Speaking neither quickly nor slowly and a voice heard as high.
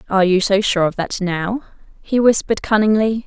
Yes: average, 185 wpm; high, 205 Hz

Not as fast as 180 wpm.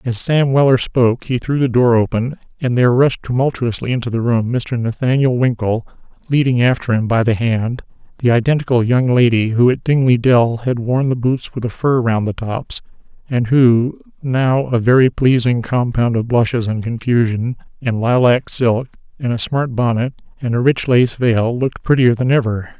No: average, 185 wpm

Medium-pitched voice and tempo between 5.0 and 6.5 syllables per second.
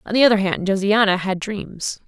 No: high, 200 Hz; 5.2 syllables/s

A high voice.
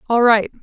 Yes: high, 230 Hz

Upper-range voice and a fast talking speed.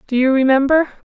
No: very high, 275 Hz; average, 160 wpm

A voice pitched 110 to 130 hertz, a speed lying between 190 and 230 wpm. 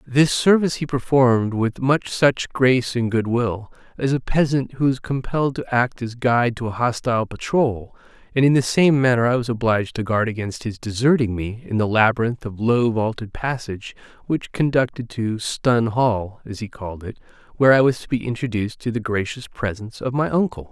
Yes: low, 120 Hz; average, 195 wpm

